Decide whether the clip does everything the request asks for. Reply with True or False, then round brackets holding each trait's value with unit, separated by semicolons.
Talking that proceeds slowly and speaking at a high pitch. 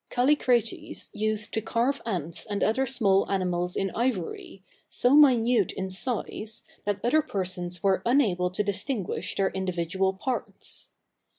True (130 wpm; 205 Hz)